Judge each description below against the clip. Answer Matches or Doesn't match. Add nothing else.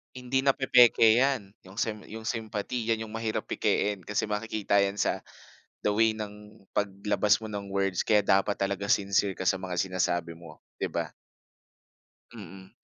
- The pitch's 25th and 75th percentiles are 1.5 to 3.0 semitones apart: Matches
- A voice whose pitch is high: Doesn't match